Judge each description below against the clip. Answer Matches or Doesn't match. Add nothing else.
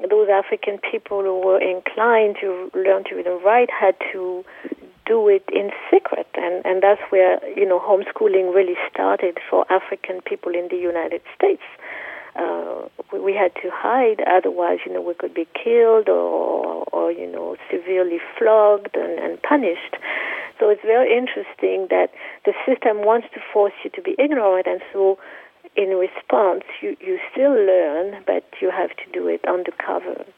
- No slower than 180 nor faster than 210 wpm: Doesn't match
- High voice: Matches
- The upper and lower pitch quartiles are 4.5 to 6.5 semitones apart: Matches